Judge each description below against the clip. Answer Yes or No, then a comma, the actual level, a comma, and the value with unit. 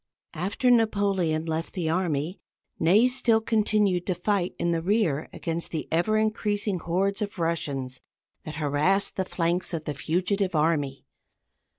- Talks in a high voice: No, medium, 180 Hz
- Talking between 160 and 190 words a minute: No, average, 145 wpm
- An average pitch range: Yes, average, 4.2 semitones